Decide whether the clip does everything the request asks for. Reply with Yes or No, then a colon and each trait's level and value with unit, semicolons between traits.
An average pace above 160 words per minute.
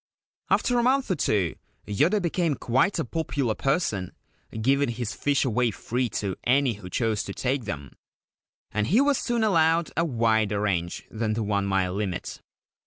Yes: average, 170 wpm